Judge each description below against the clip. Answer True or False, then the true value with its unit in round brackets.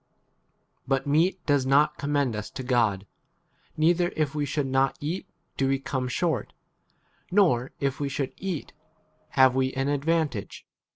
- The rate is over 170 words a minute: False (155 wpm)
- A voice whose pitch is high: False (140 Hz)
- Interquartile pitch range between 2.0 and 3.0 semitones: True (2.7 semitones)